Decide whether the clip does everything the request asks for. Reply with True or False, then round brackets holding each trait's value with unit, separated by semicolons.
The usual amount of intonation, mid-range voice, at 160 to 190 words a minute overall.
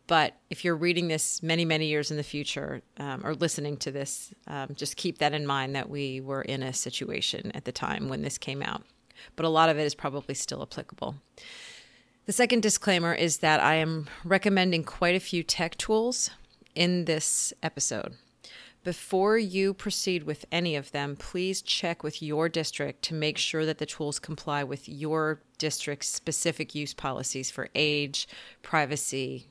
True (3.4 semitones; 155 Hz; 180 wpm)